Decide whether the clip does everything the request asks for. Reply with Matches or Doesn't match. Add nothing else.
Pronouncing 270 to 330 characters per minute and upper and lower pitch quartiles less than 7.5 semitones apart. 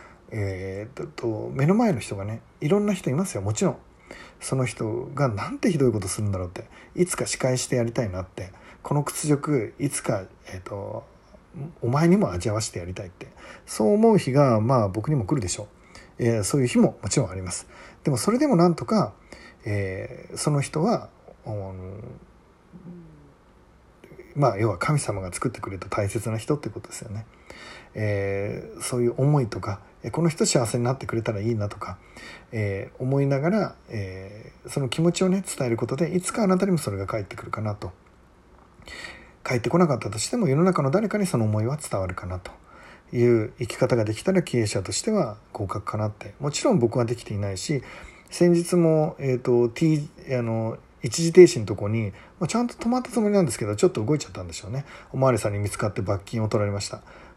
Doesn't match